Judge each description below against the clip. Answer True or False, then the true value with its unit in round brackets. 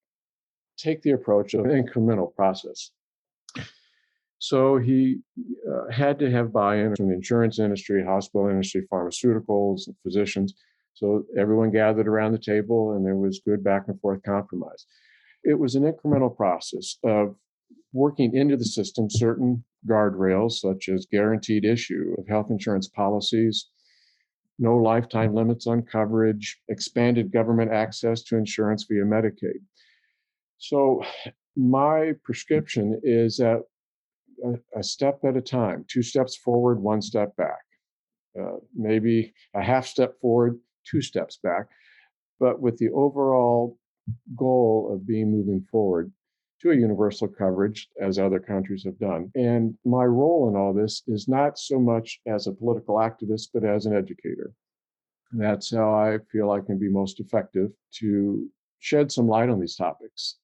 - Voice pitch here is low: True (110 Hz)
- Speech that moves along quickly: False (145 wpm)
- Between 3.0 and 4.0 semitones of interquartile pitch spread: True (3.3 semitones)